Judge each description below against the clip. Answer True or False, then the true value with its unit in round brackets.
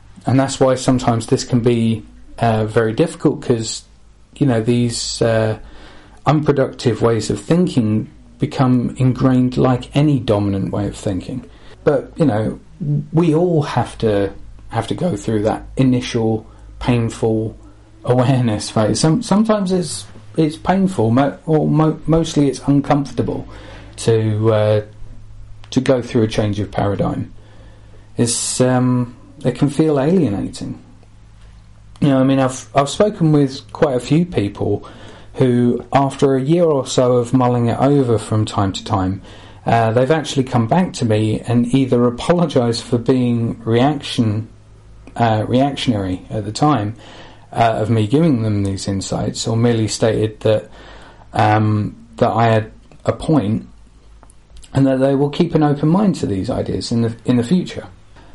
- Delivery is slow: False (150 wpm)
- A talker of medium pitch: False (120 Hz)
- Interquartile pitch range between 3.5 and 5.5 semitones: True (4.0 semitones)